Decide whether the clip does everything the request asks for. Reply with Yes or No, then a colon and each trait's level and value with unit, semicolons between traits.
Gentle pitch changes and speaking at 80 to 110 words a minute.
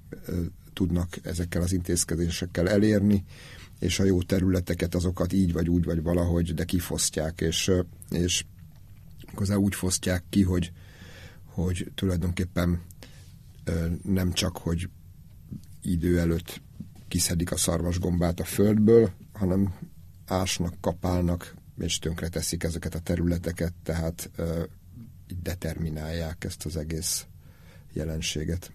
Yes: narrow, 1.8 semitones; slow, 105 wpm